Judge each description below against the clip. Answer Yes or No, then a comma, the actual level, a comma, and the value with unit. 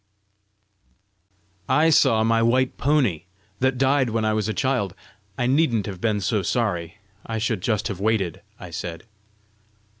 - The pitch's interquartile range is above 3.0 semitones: Yes, average, 4.4 semitones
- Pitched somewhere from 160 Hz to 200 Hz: No, low, 110 Hz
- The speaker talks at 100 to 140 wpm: No, average, 150 wpm